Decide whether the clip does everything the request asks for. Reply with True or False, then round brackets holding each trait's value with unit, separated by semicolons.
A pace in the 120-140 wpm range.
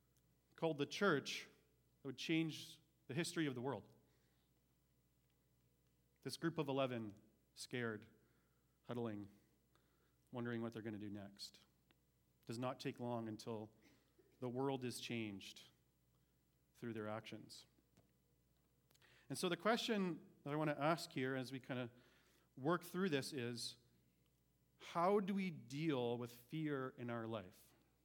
True (135 wpm)